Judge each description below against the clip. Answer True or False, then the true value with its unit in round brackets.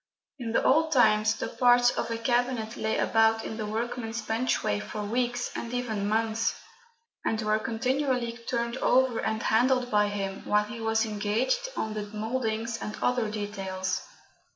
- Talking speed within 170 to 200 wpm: False (160 wpm)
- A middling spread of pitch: False (2.3 semitones)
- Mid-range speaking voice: False (225 Hz)